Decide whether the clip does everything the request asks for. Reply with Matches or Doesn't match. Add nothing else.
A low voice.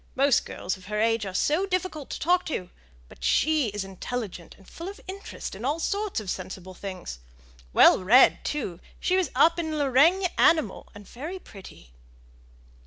Doesn't match